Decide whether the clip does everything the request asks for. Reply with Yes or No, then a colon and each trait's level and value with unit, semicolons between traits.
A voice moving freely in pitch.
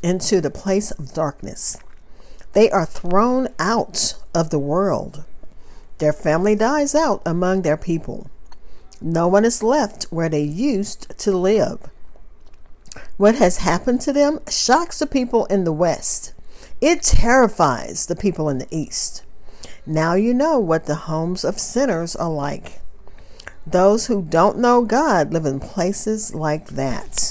Yes: wide, 5.9 semitones